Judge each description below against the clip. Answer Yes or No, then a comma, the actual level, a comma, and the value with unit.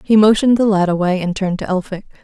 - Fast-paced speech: Yes, fast, 240 wpm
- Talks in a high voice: Yes, high, 195 Hz